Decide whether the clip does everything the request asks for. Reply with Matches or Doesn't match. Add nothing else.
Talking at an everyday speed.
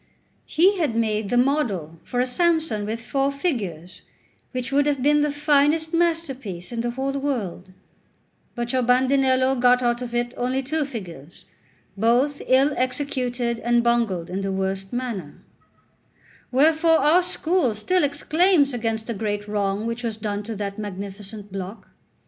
Matches